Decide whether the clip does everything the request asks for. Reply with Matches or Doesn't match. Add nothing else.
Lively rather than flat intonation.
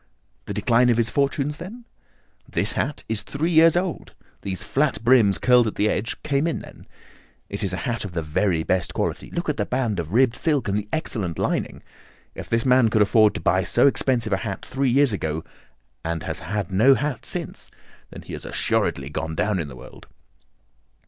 Matches